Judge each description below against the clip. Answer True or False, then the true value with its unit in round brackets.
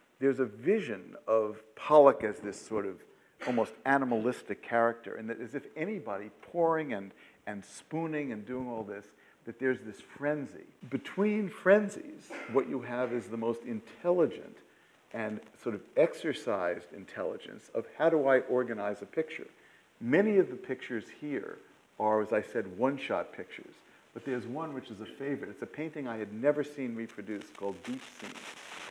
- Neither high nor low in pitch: False (125 Hz)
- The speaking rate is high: False (165 wpm)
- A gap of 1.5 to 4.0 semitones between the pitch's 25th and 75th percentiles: False (5.1 semitones)